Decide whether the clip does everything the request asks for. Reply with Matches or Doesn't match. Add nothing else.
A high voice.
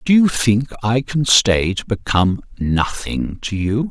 Doesn't match